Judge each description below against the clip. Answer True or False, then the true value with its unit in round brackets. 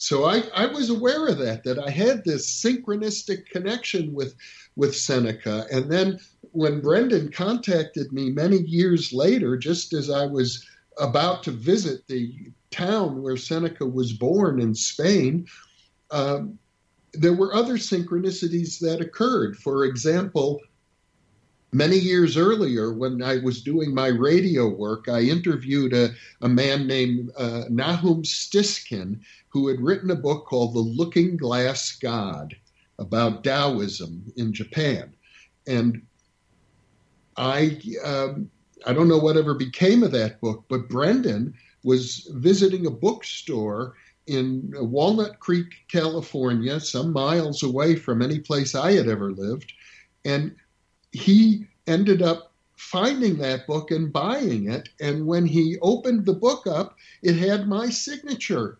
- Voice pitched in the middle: True (150 Hz)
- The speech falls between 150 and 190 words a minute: False (135 wpm)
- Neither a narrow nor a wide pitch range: False (6.3 semitones)